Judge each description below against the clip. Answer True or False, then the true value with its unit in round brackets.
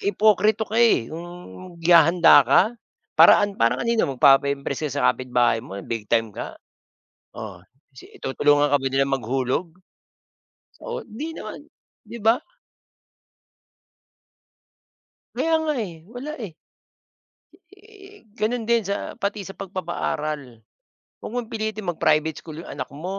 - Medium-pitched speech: True (175 Hz)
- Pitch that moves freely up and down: True (7.7 semitones)